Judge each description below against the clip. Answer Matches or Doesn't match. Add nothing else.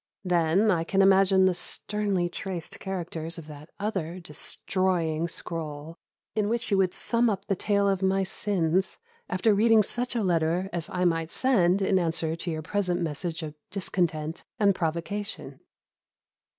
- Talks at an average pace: Matches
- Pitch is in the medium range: Matches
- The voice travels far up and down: Doesn't match